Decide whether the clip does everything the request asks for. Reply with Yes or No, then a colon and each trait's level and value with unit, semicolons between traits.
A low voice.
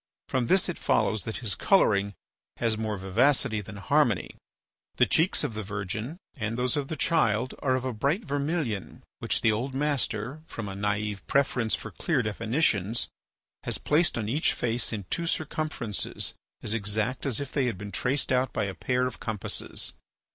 Yes: low, 120 Hz